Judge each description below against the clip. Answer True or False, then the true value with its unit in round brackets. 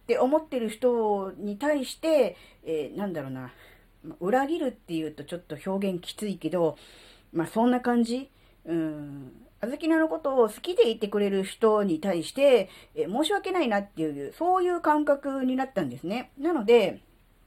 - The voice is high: True (210 Hz)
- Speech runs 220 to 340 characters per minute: True (320 characters per minute)